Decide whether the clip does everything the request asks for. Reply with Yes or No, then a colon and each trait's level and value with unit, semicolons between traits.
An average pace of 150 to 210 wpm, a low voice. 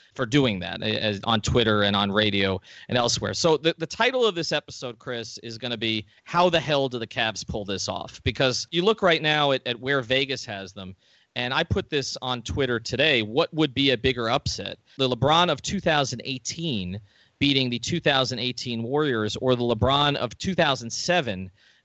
Yes: average, 190 wpm; low, 125 Hz